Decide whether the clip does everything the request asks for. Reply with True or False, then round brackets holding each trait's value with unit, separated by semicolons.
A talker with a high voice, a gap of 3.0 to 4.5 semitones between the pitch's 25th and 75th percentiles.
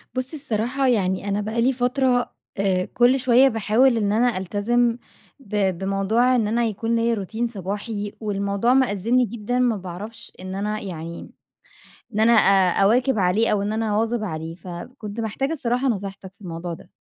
True (215 Hz; 3.6 semitones)